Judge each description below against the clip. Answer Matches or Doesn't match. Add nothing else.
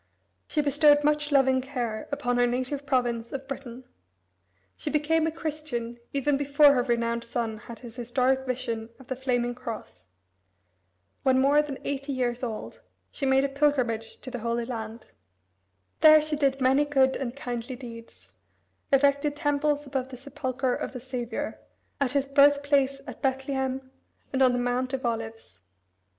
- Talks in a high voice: Matches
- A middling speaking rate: Matches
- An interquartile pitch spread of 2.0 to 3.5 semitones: Matches